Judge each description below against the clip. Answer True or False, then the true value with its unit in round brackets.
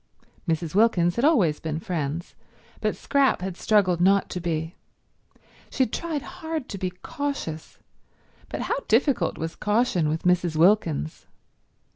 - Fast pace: False (140 wpm)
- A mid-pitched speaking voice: True (180 Hz)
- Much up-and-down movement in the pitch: True (6.7 semitones)